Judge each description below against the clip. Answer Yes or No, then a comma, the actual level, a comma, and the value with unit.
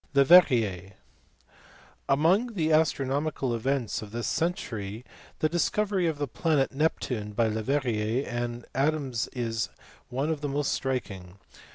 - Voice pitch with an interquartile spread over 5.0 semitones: Yes, wide, 5.4 semitones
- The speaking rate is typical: No, slow, 125 wpm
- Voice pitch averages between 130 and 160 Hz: Yes, low, 135 Hz